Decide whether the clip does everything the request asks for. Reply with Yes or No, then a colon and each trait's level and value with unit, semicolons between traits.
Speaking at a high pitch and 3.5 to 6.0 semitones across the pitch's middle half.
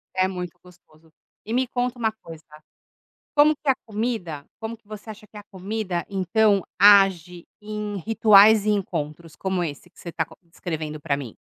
Yes: high, 195 Hz; average, 4.1 semitones